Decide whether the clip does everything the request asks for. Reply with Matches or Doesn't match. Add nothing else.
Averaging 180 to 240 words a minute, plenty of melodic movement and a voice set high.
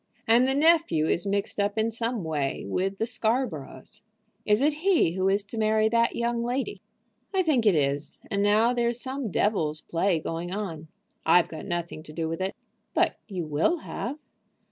Matches